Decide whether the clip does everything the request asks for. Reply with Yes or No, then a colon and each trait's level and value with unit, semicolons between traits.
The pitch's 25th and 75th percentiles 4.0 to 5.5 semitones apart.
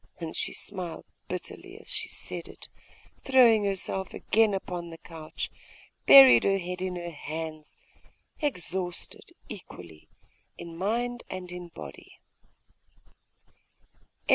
No: average, 3.2 semitones